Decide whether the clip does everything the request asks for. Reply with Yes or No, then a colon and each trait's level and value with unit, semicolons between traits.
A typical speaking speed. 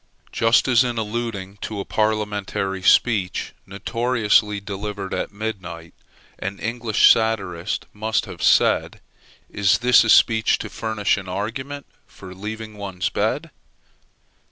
No: slow, 125 wpm